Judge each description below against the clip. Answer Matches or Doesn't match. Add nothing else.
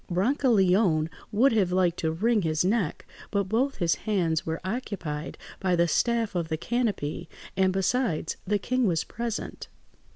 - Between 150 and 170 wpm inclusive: Matches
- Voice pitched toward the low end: Doesn't match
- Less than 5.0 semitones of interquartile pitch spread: Doesn't match